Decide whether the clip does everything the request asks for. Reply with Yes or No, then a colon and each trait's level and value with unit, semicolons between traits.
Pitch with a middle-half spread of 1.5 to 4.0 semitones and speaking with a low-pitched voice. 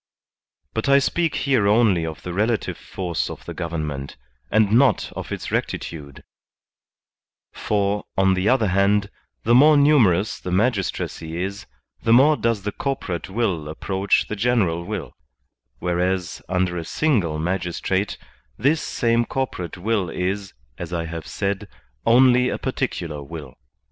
No: average, 5.1 semitones; low, 100 Hz